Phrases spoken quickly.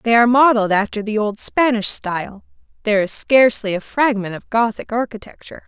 No: average, 170 wpm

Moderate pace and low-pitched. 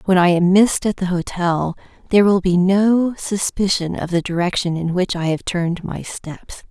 No: average, 195 wpm; medium, 185 Hz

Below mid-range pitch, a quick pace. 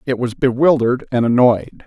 No: low, 125 Hz; average, 160 wpm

